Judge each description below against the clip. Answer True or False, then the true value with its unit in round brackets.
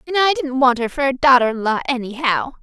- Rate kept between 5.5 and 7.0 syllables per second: True (6.0 syllables/s)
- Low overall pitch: False (260 Hz)